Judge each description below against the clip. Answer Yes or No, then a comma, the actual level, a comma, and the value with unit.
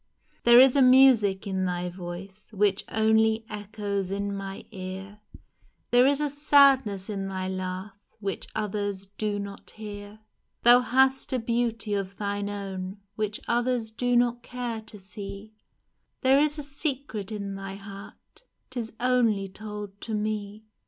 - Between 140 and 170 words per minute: Yes, average, 150 wpm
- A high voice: Yes, high, 210 Hz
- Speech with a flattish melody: No, average, 3.4 semitones